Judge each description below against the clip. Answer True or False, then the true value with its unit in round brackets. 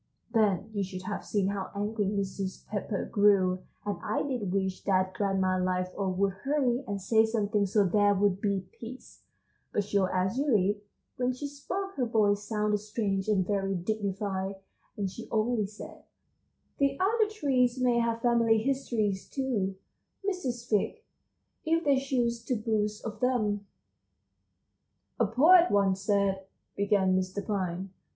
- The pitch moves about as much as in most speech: True (3.6 semitones)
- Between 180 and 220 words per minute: False (150 wpm)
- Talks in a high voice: True (210 Hz)